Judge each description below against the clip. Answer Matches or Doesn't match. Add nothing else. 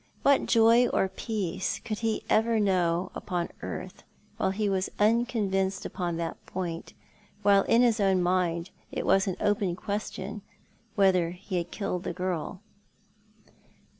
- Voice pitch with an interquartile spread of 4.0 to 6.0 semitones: Doesn't match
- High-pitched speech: Matches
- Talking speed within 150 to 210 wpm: Doesn't match